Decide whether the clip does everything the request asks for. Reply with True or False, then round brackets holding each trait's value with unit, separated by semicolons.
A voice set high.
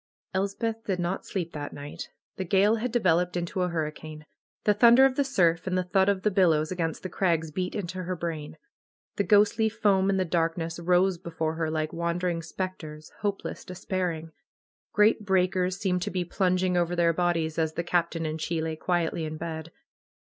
False (180 Hz)